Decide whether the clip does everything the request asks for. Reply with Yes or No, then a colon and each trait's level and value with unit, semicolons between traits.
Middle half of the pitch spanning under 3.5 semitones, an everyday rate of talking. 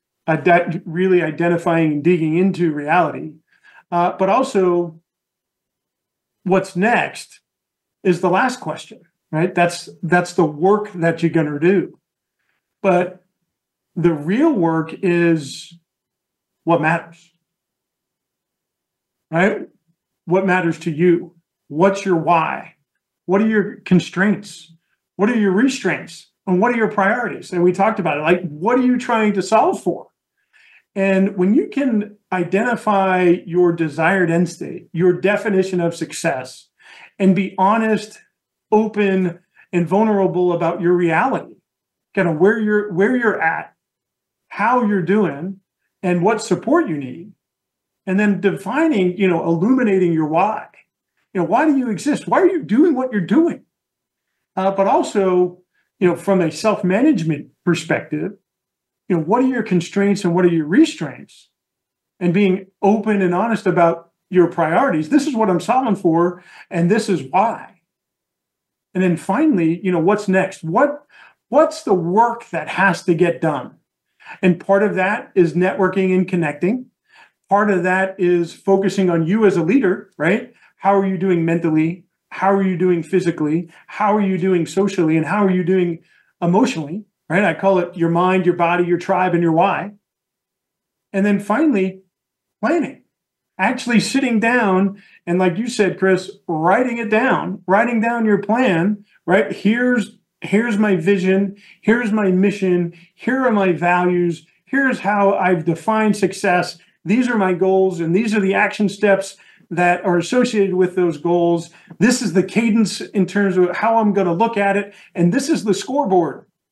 Yes: average, 3.1 semitones; average, 155 wpm